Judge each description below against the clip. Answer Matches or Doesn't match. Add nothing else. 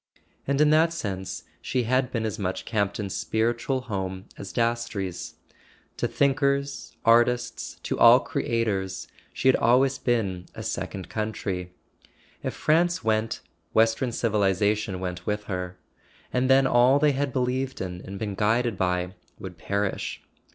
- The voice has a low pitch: Matches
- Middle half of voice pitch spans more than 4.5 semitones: Matches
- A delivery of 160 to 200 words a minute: Doesn't match